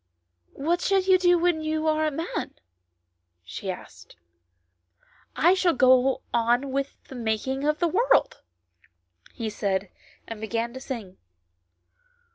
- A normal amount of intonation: No, wide, 7.2 semitones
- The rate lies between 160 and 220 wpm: No, average, 145 wpm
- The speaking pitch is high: Yes, very high, 260 Hz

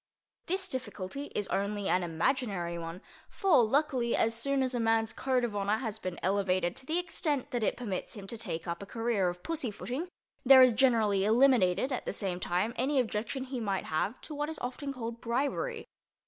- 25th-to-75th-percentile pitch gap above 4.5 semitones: Yes, average, 5.1 semitones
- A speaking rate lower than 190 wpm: No, average, 195 wpm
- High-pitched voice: Yes, high, 230 Hz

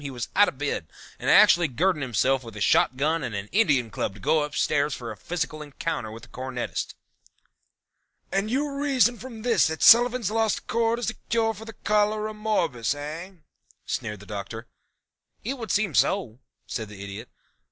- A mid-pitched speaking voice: Yes, medium, 155 Hz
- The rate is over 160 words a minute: Yes, average, 175 wpm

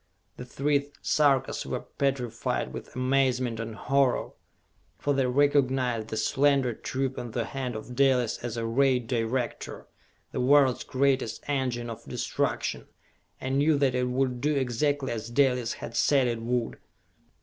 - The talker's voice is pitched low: Yes, low, 130 Hz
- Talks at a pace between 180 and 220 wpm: No, average, 150 wpm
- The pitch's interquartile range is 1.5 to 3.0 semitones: Yes, narrow, 2.4 semitones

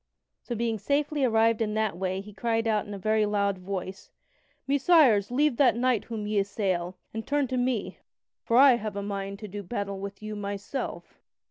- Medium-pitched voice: No, high, 215 Hz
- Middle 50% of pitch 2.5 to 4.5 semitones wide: Yes, average, 3.3 semitones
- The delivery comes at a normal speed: Yes, average, 195 wpm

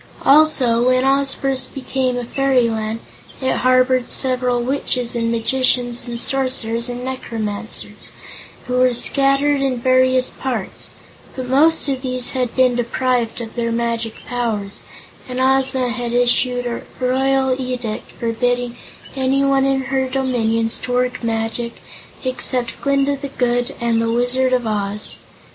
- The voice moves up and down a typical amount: No, narrow, 1.9 semitones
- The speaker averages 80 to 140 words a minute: Yes, slow, 135 wpm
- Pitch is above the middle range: Yes, very high, 250 Hz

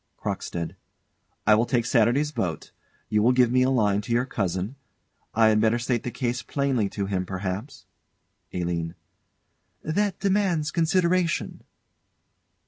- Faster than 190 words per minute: No, slow, 135 wpm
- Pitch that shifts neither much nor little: No, wide, 5.7 semitones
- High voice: No, low, 120 Hz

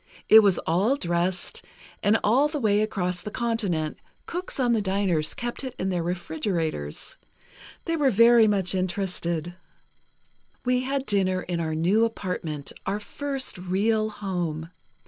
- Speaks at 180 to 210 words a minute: No, average, 145 wpm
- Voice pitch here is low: No, high, 195 Hz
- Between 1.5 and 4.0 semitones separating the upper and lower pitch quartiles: No, average, 4.7 semitones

